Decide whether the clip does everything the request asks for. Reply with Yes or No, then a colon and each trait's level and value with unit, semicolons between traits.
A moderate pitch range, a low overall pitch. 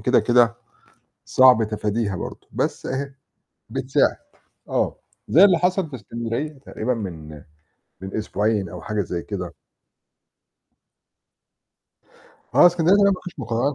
No: wide, 6.5 semitones; low, 120 Hz